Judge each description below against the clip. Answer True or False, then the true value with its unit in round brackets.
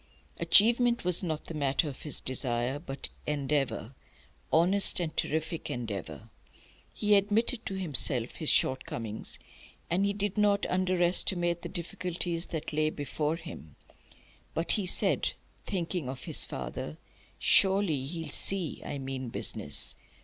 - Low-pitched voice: False (165 Hz)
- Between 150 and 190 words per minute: False (135 wpm)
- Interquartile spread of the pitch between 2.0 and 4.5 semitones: False (5.5 semitones)